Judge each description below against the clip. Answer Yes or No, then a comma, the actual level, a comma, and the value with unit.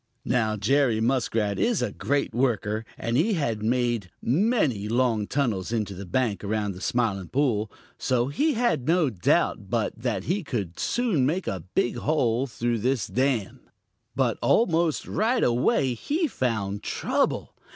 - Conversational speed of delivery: Yes, average, 150 wpm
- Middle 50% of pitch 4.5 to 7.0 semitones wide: Yes, average, 5.0 semitones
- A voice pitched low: Yes, low, 120 Hz